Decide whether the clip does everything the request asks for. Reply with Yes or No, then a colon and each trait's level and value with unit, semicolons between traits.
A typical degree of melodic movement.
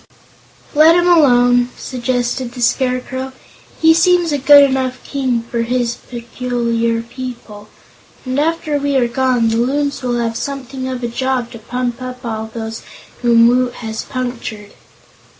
No: narrow, 2.1 semitones